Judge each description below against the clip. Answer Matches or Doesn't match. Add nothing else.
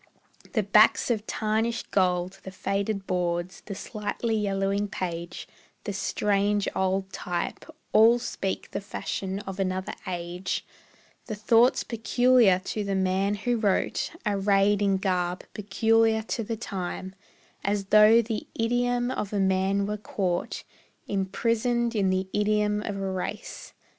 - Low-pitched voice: Doesn't match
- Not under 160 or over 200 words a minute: Doesn't match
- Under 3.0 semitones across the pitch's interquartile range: Matches